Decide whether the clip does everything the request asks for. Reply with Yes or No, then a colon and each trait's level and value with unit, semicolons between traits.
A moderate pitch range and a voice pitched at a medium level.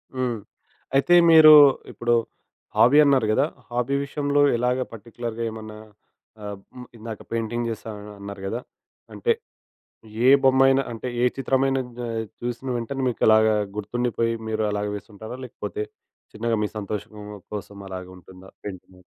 No: average, 3.4 semitones; low, 115 Hz